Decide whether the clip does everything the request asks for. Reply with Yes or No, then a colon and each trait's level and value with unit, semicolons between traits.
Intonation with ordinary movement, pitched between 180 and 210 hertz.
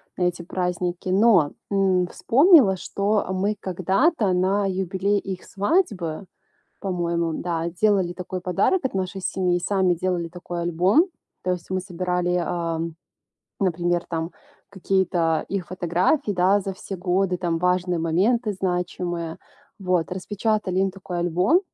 No: narrow, 1.9 semitones; medium, 185 Hz